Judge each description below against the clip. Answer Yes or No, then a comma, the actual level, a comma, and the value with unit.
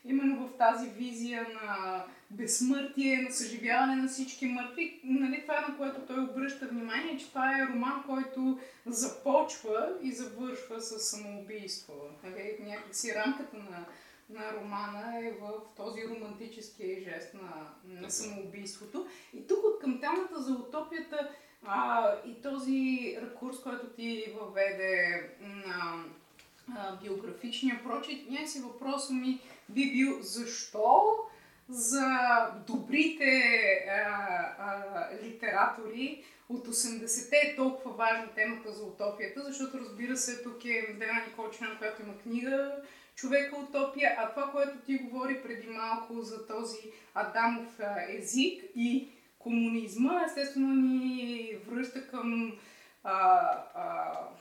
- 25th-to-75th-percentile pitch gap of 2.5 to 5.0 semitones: Yes, average, 3.7 semitones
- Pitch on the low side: No, high, 240 Hz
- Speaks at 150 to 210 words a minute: No, average, 120 wpm